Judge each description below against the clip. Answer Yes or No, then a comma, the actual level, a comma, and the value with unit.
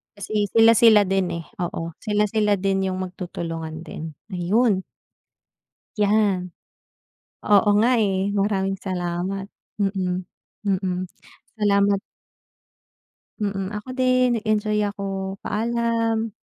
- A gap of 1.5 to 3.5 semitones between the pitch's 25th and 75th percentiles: Yes, narrow, 2.4 semitones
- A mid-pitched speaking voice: No, high, 200 Hz